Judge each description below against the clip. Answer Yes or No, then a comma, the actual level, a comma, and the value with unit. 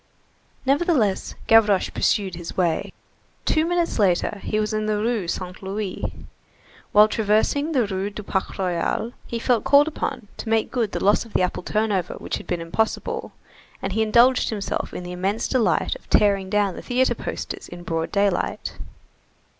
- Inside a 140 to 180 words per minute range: Yes, average, 170 wpm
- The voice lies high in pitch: Yes, high, 210 Hz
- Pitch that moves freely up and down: No, average, 3.5 semitones